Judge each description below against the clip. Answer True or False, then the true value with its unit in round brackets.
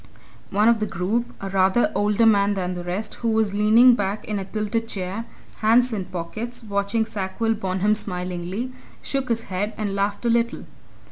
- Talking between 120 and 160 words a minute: False (180 wpm)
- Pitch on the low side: False (210 Hz)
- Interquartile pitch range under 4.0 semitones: True (2.9 semitones)